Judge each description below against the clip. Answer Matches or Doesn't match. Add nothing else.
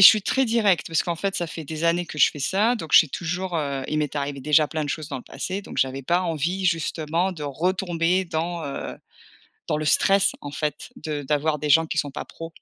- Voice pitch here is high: Doesn't match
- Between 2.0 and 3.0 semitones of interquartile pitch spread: Doesn't match